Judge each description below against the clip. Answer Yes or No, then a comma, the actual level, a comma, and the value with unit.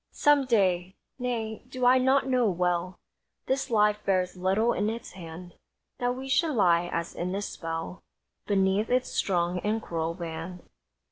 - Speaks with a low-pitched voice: No, high, 195 Hz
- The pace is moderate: Yes, average, 155 wpm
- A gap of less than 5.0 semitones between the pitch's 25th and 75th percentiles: No, wide, 5.6 semitones